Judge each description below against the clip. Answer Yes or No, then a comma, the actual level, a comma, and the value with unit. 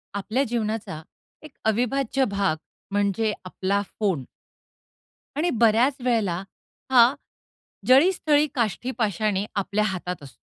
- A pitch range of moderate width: Yes, average, 4.2 semitones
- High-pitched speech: Yes, high, 220 Hz